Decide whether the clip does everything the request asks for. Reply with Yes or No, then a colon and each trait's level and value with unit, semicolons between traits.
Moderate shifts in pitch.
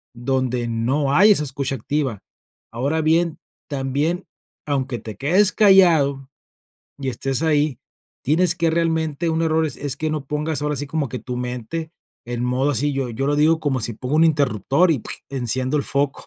Yes: average, 3.6 semitones